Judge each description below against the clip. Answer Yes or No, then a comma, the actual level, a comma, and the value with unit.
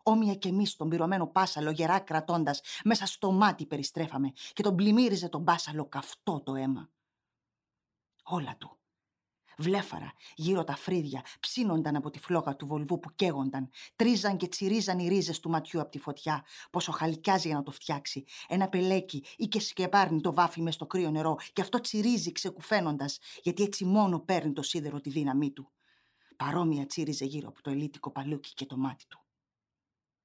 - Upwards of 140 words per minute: Yes, fast, 170 wpm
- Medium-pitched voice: Yes, medium, 165 Hz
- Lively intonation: No, average, 4.5 semitones